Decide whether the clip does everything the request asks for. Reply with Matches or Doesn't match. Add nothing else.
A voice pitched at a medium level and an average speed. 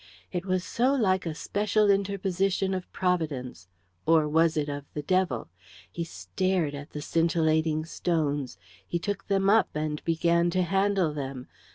Matches